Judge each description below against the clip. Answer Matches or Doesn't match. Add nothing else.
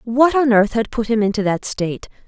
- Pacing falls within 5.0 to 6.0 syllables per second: Matches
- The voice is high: Matches